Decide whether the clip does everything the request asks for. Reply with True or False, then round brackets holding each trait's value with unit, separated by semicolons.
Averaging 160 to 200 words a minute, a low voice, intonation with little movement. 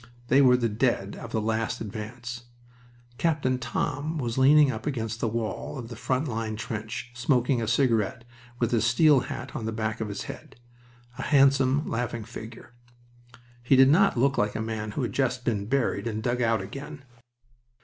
False (180 wpm; 120 Hz; 3.0 semitones)